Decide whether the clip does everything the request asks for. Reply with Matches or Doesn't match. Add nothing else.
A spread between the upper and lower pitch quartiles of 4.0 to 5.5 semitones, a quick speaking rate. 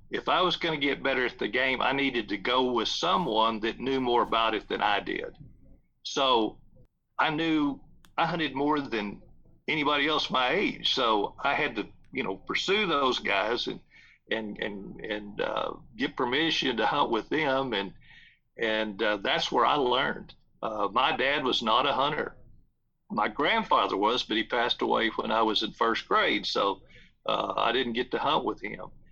Doesn't match